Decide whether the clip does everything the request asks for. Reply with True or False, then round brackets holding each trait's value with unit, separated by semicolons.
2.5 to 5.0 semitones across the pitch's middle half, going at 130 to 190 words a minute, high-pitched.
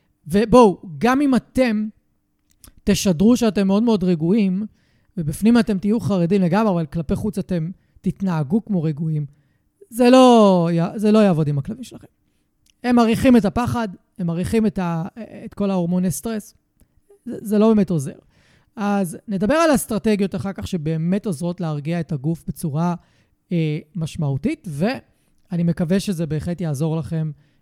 True (4.3 semitones; 140 wpm; 195 Hz)